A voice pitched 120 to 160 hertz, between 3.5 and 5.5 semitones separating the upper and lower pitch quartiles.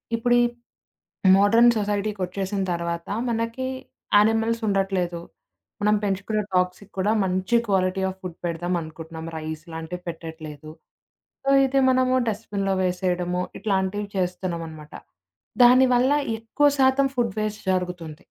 No: high, 190 Hz; average, 3.9 semitones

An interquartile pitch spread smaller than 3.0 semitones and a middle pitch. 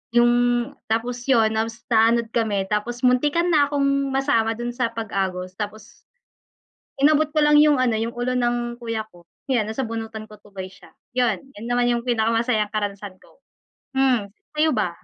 No: narrow, 2.6 semitones; high, 235 Hz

